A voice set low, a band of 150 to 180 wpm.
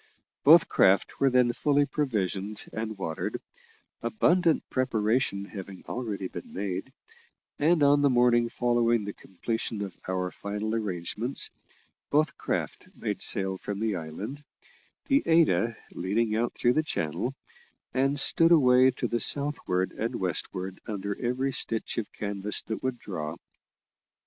No: low, 115 Hz; slow, 135 wpm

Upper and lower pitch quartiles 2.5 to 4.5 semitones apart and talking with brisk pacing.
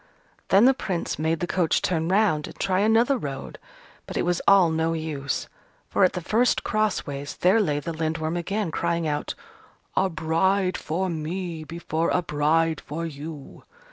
No: average, 3.2 semitones; average, 170 wpm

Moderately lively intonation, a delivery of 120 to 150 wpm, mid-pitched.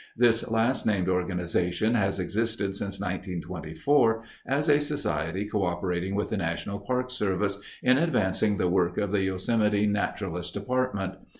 No: average, 3.6 semitones; slow, 135 wpm; low, 100 Hz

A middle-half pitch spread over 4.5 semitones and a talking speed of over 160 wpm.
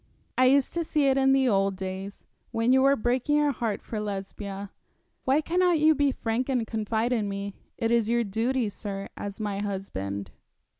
Yes: average, 5.0 semitones; average, 190 wpm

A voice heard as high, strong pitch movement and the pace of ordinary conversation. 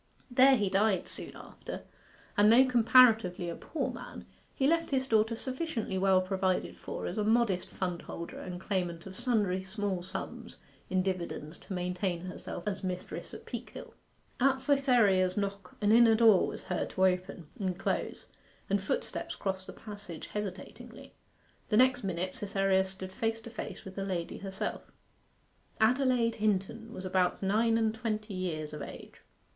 No: high, 200 Hz; average, 3.6 semitones; average, 160 wpm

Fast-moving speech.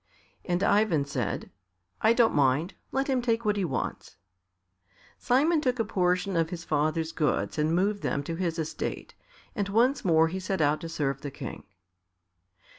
No: average, 170 wpm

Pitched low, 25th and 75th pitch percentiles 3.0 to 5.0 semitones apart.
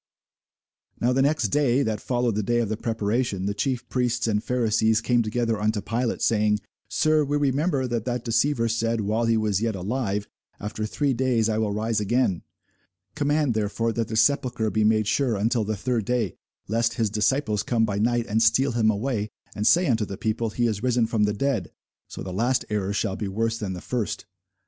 No: low, 115 Hz; narrow, 2.6 semitones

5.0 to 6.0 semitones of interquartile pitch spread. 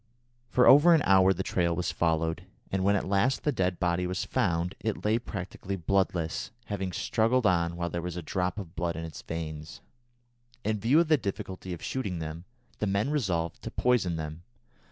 No: average, 3.8 semitones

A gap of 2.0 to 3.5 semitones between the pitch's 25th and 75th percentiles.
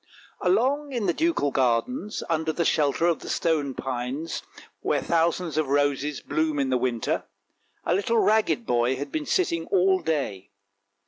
No: average, 5.1 semitones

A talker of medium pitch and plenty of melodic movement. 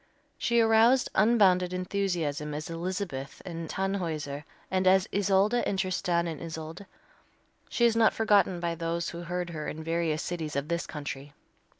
No: medium, 175 Hz; average, 3.5 semitones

